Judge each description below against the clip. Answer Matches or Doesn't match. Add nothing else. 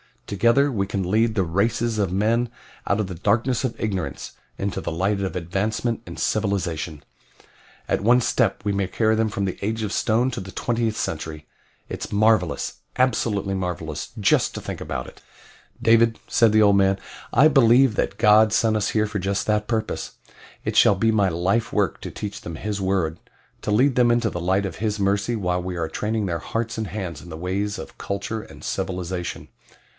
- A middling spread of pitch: Matches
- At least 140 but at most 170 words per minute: Doesn't match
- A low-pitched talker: Matches